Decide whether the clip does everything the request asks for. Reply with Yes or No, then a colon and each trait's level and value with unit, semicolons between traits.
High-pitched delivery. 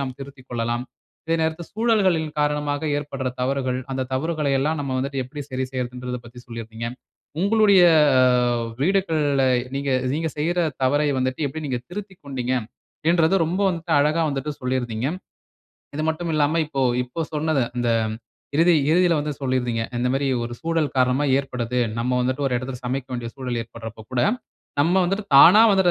No: medium, 140 Hz